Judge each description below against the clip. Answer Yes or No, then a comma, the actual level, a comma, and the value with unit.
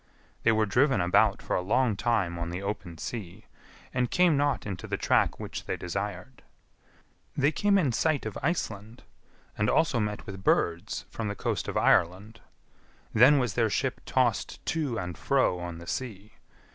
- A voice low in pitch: Yes, low, 110 Hz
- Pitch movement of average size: No, wide, 5.9 semitones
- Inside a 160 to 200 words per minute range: Yes, average, 170 wpm